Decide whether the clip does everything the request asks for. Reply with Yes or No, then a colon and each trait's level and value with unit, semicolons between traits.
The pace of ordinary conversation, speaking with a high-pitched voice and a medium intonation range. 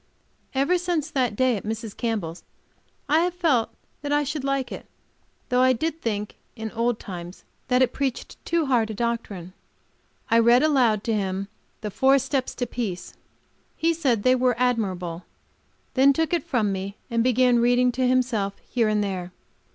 Yes: average, 175 wpm; high, 245 Hz; average, 4.1 semitones